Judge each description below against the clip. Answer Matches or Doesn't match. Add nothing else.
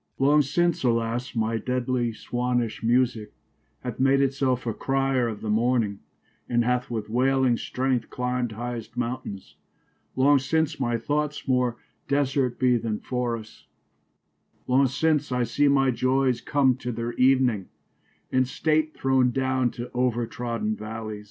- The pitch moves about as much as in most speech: Doesn't match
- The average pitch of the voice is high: Doesn't match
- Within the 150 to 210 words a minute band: Matches